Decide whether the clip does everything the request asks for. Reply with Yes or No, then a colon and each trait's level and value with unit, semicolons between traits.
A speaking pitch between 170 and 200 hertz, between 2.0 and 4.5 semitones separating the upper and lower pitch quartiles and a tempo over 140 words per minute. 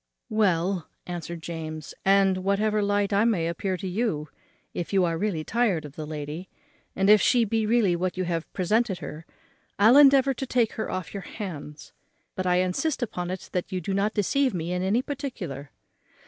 Yes: high, 190 Hz; average, 4.0 semitones; average, 190 wpm